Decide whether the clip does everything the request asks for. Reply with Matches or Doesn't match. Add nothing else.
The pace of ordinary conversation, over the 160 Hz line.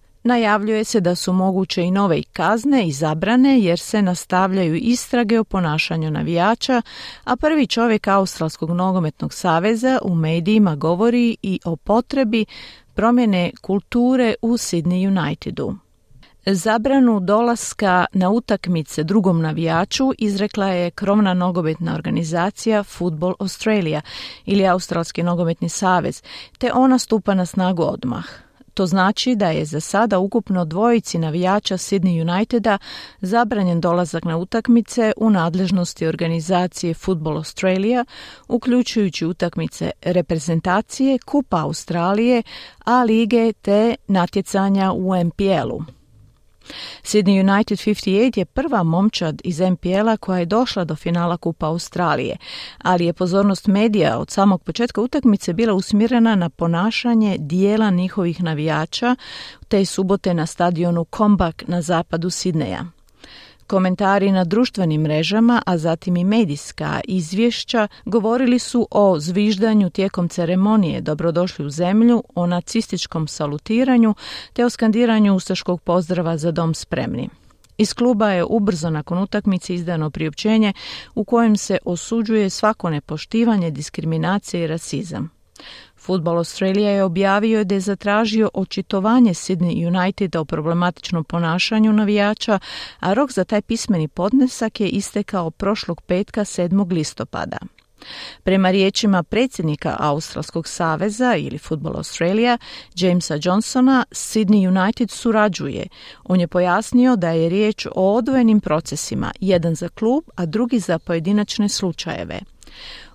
Matches